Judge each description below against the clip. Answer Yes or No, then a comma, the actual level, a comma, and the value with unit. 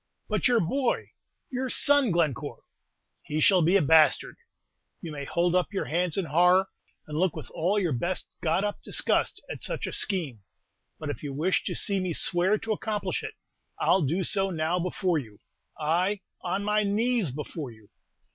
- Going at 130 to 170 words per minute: No, average, 180 wpm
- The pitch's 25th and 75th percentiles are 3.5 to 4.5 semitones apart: Yes, average, 4.2 semitones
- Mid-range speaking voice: Yes, medium, 180 Hz